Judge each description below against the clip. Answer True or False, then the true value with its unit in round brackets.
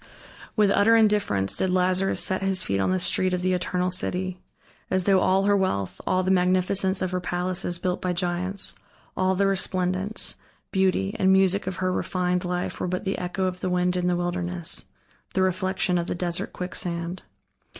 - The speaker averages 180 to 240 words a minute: True (185 wpm)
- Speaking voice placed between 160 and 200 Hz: True (185 Hz)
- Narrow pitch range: True (1.0 semitones)